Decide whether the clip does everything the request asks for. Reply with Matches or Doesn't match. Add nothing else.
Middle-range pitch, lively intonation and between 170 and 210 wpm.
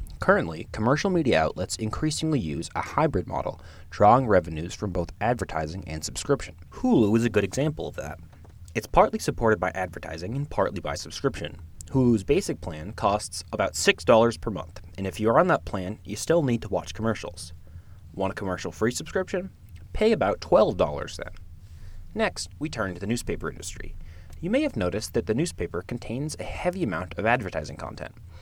Doesn't match